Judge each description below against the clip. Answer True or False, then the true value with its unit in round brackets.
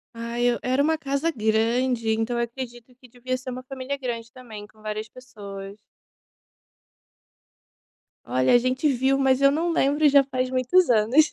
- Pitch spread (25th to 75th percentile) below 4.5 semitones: True (2.8 semitones)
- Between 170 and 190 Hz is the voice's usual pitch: False (255 Hz)